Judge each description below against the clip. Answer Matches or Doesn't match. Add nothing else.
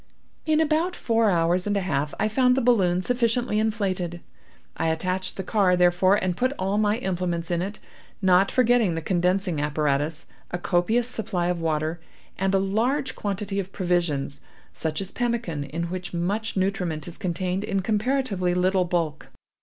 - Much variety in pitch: Doesn't match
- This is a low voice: Doesn't match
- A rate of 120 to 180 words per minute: Matches